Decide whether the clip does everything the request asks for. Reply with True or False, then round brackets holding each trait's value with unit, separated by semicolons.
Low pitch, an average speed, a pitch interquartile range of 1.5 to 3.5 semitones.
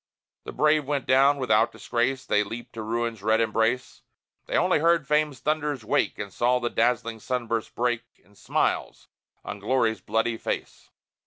True (120 Hz; 160 wpm; 3.2 semitones)